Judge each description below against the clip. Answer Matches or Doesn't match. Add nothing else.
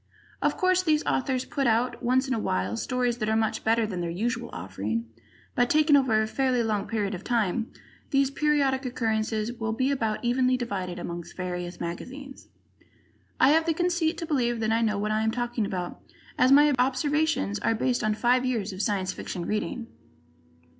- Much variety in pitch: Doesn't match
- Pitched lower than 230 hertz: Doesn't match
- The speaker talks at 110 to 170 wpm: Doesn't match